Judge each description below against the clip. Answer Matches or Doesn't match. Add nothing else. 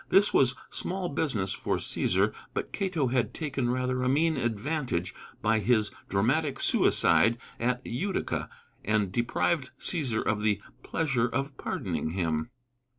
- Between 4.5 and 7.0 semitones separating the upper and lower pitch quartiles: Matches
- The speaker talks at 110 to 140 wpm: Matches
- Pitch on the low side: Matches